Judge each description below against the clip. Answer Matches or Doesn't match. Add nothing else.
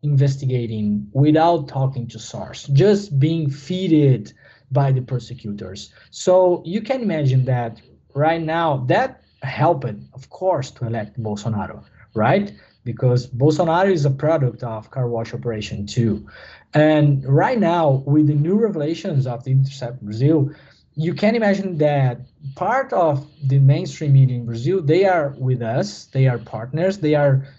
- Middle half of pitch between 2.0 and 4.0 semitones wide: Doesn't match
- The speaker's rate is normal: Matches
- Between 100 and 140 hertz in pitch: Matches